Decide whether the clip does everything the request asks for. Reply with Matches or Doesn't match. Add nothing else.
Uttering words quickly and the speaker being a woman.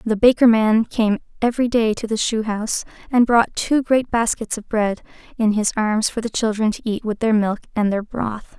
Matches